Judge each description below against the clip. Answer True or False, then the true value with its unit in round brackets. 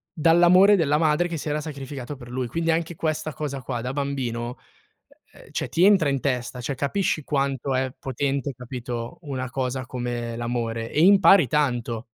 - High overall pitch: False (135 Hz)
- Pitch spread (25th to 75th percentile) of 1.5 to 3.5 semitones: False (4.1 semitones)